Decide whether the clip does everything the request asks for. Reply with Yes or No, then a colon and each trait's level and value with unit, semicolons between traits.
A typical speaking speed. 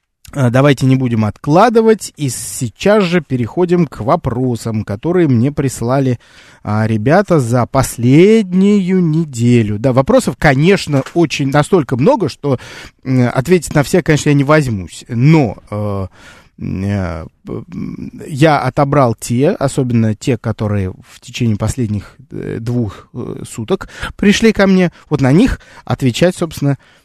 Yes: average, 125 wpm